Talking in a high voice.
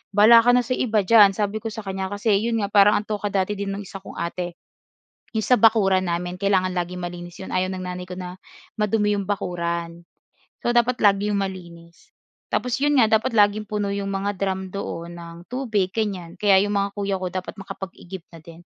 Yes: high, 195 Hz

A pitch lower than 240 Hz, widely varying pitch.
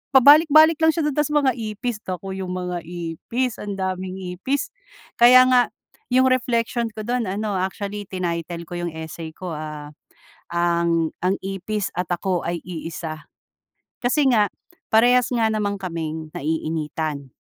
Yes: high, 190 Hz; wide, 6.2 semitones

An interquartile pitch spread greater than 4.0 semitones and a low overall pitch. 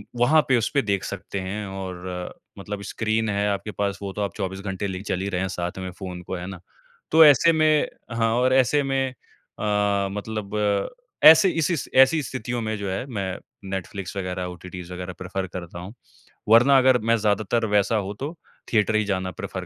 Yes: average, 4.4 semitones; low, 100 Hz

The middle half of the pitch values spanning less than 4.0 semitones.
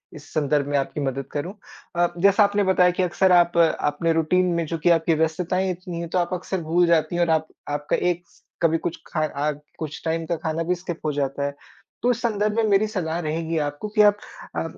Yes: average, 2.9 semitones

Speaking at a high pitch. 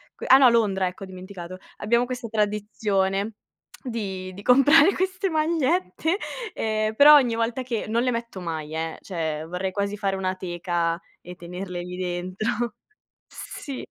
Yes: high, 200 Hz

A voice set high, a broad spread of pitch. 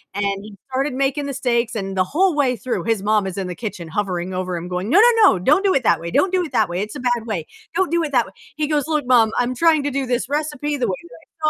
Yes: high, 245 Hz; wide, 7.1 semitones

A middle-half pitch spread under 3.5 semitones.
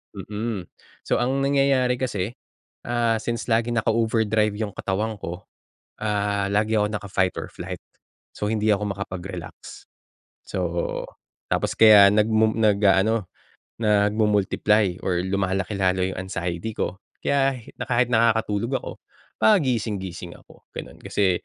Yes: average, 2.8 semitones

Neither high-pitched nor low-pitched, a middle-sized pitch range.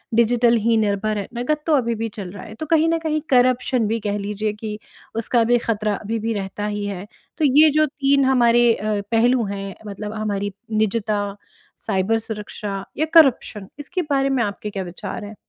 No: high, 220 Hz; average, 3.6 semitones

